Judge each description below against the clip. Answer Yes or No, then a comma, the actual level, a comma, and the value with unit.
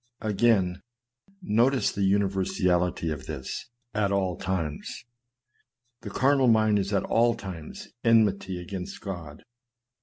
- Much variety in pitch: No, average, 3.5 semitones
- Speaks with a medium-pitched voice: No, very low, 95 Hz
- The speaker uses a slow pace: Yes, slow, 115 wpm